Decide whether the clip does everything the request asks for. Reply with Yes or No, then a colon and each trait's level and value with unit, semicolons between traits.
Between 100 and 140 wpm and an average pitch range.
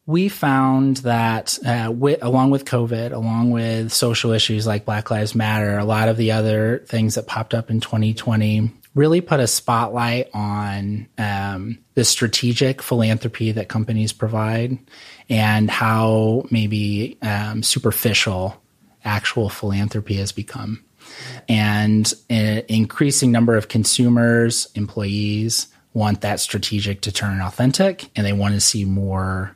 No: slow, 135 wpm; narrow, 2.0 semitones